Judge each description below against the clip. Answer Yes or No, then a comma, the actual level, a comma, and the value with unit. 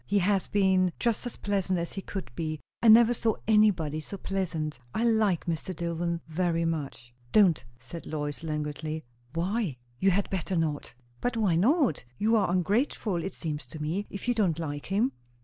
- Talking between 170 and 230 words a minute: Yes, average, 180 wpm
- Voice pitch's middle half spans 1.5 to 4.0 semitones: No, average, 4.6 semitones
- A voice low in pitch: No, medium, 180 Hz